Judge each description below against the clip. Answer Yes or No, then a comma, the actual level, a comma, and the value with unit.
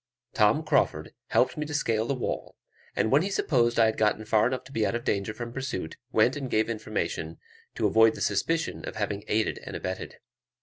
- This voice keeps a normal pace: No, fast, 210 wpm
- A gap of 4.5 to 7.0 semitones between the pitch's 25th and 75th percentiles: No, average, 3.6 semitones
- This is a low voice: Yes, low, 115 Hz